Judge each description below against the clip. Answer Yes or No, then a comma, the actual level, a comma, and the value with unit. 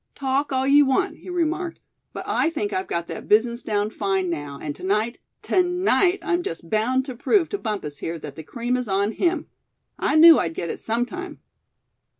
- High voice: Yes, high, 240 Hz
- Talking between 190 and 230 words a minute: Yes, average, 200 wpm